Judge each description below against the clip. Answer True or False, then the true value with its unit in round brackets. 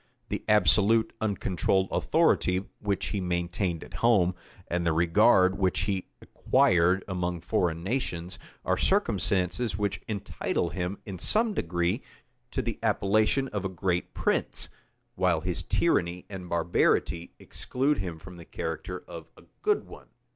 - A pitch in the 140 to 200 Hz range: False (90 Hz)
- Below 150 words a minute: True (140 wpm)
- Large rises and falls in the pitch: False (2.7 semitones)